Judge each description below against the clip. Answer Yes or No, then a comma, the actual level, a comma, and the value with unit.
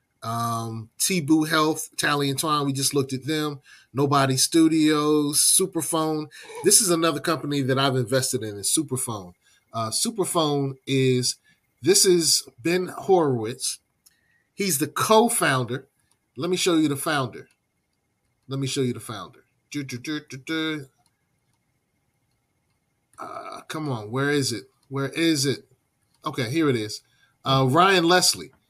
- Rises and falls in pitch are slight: No, average, 3.7 semitones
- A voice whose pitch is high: No, medium, 140 Hz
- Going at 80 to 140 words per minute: Yes, slow, 135 wpm